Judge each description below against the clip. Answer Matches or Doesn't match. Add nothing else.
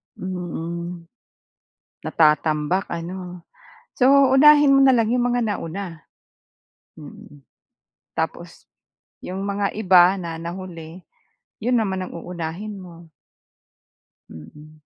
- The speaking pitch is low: Doesn't match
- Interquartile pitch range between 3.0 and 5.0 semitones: Matches